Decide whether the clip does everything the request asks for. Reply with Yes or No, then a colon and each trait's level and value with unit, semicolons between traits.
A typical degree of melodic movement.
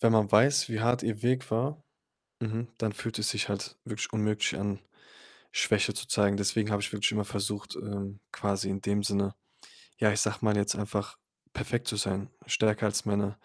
No: narrow, 1.7 semitones